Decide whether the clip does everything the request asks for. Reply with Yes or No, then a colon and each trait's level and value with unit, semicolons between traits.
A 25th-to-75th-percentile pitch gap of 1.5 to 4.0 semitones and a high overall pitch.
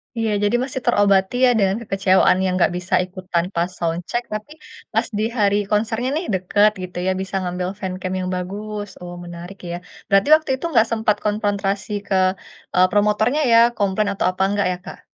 Yes: narrow, 2.5 semitones; high, 200 Hz